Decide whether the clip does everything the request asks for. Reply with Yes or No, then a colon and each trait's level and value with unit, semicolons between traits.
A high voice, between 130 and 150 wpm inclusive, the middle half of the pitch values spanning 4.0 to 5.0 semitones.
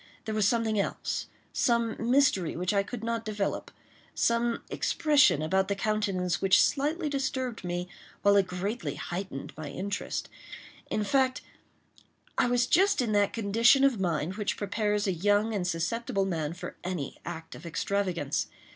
Yes: high, 205 Hz; average, 145 wpm; average, 4.3 semitones